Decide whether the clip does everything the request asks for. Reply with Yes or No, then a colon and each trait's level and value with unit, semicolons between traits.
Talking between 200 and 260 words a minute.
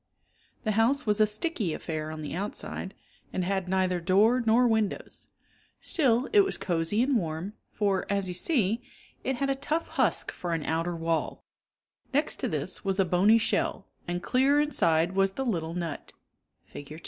No: average, 170 wpm